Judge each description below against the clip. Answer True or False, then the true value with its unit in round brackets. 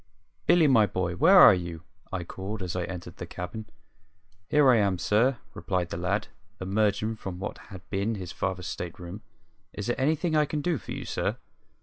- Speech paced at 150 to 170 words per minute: False (195 wpm)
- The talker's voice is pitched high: False (100 Hz)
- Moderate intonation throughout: True (4.9 semitones)